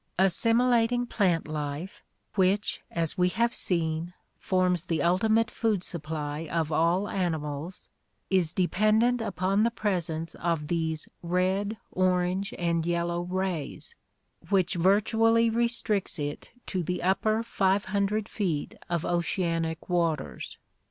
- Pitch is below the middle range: No, medium, 180 Hz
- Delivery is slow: Yes, slow, 120 wpm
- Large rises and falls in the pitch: No, average, 3.7 semitones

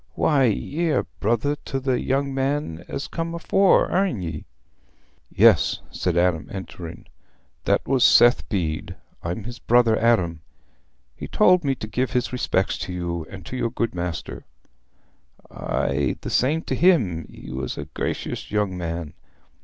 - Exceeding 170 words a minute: No, average, 145 wpm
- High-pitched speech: No, low, 115 Hz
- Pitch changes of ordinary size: No, wide, 7.8 semitones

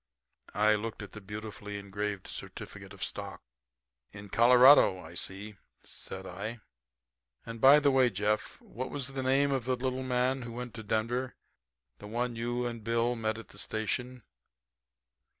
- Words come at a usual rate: Yes, average, 160 wpm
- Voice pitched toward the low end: Yes, low, 115 Hz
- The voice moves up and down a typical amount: Yes, average, 3.3 semitones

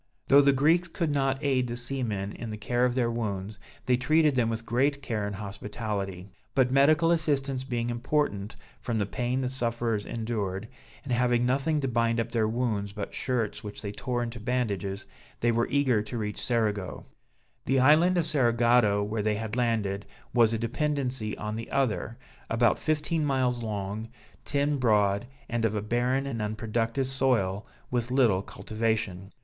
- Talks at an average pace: Yes, average, 170 wpm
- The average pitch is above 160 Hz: No, low, 120 Hz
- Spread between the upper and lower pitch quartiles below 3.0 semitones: No, average, 3.7 semitones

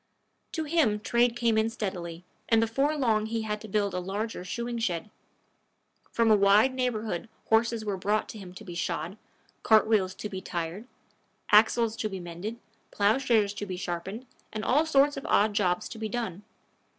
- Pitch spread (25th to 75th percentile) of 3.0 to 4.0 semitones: Yes, average, 3.3 semitones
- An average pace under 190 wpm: Yes, average, 175 wpm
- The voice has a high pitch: Yes, high, 215 Hz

